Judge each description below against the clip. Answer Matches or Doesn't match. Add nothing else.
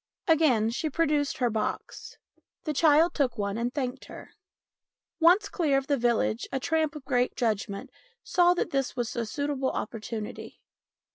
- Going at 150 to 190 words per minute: Matches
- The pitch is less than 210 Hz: Doesn't match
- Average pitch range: Matches